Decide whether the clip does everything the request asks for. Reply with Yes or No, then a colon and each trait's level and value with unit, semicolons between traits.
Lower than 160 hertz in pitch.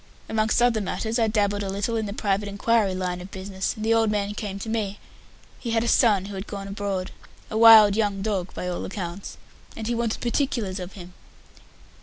No: high, 205 Hz